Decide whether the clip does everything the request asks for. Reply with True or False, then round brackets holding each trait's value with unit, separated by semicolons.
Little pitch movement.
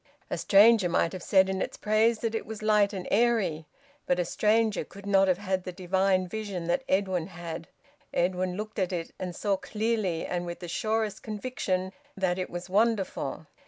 False (3.0 semitones)